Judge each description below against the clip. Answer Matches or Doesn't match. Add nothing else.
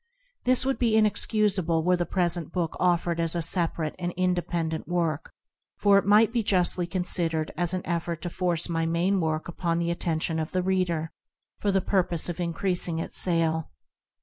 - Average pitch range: Doesn't match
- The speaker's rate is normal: Matches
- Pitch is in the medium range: Matches